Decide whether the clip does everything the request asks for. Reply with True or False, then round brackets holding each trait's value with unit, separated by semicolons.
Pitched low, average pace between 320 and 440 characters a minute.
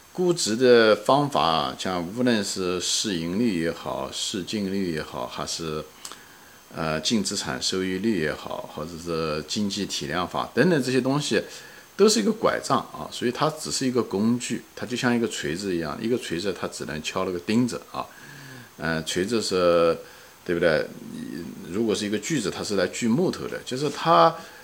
False (105 Hz; 260 characters per minute)